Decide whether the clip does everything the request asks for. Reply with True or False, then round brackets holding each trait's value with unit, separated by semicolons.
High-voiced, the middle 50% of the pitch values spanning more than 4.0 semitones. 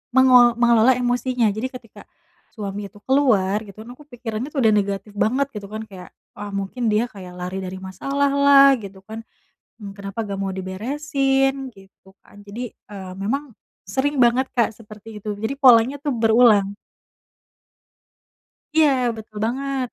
True (225 Hz; 4.6 semitones)